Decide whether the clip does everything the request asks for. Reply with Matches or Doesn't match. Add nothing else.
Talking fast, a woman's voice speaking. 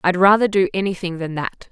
Matches